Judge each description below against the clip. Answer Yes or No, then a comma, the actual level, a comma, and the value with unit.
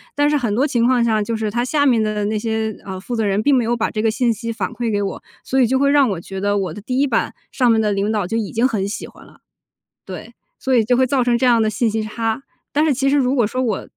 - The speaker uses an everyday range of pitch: Yes, average, 3.2 semitones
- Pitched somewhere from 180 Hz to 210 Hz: No, high, 230 Hz